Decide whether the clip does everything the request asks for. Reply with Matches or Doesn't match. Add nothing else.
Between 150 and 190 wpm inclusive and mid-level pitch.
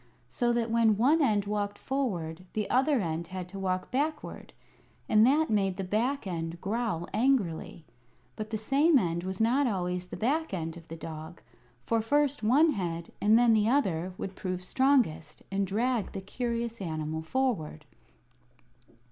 Doesn't match